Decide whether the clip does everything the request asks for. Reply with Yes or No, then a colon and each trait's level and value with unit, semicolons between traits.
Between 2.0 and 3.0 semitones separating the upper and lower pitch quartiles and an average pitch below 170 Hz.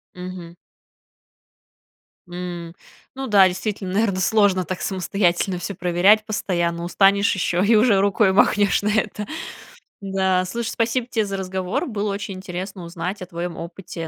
No: narrow, 2.5 semitones; high, 190 Hz